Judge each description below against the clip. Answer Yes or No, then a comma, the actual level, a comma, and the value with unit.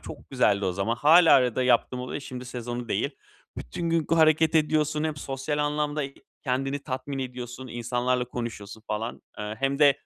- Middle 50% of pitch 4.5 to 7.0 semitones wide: No, average, 3.5 semitones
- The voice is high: No, low, 130 Hz